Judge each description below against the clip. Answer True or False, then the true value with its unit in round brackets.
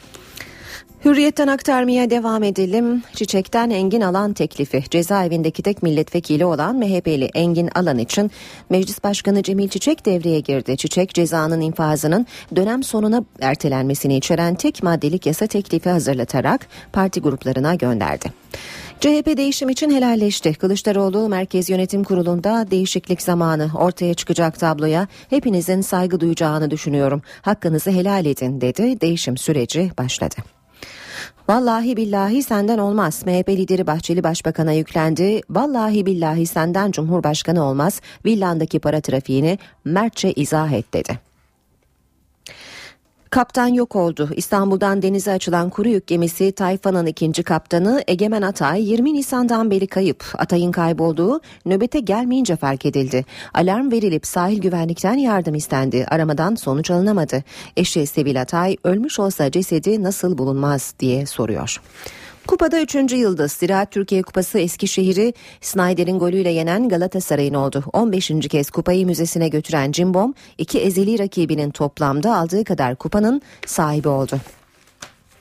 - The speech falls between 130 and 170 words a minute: False (120 wpm)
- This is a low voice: False (180 Hz)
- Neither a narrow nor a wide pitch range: True (4.6 semitones)